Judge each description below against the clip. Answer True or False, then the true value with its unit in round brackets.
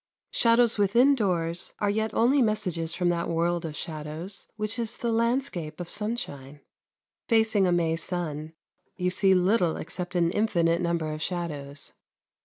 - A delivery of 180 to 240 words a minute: False (150 wpm)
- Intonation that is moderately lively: True (4.8 semitones)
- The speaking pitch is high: False (180 Hz)